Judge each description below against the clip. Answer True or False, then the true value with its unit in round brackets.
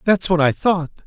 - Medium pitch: True (170 Hz)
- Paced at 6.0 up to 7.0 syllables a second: False (5.0 syllables/s)